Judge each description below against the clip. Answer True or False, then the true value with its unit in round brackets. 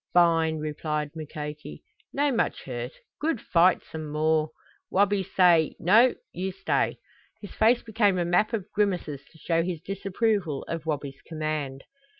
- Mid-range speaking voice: True (165 Hz)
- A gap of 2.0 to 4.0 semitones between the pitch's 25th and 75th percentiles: False (4.5 semitones)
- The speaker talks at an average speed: True (145 wpm)